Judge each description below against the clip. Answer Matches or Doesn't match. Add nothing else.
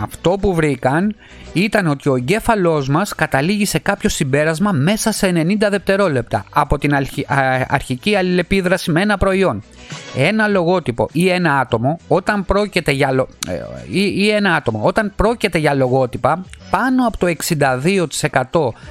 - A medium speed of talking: Matches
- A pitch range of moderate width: Doesn't match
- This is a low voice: Doesn't match